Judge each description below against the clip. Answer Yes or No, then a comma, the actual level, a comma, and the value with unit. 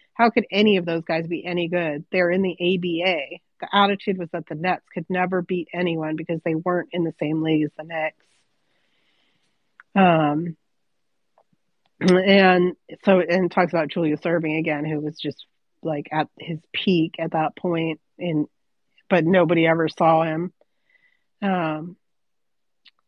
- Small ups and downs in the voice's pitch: Yes, narrow, 2.3 semitones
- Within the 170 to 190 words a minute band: No, average, 155 wpm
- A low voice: No, medium, 170 Hz